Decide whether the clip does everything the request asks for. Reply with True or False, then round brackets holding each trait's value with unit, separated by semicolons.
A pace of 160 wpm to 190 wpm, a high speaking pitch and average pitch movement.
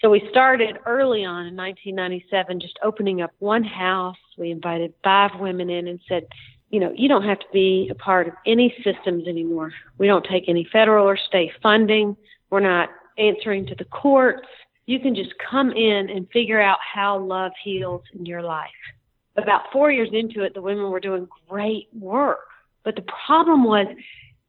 True (185 wpm; 195 Hz; 3.1 semitones)